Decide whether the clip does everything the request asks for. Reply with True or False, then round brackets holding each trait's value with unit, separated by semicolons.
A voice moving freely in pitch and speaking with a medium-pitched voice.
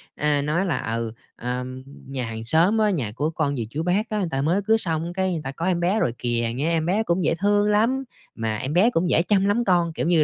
True (6.3 semitones; 165 Hz)